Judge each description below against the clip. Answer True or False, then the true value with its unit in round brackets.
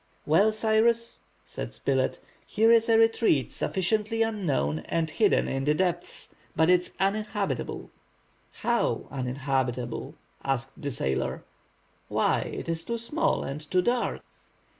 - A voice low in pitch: False (180 Hz)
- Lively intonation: True (8.5 semitones)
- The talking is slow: True (130 wpm)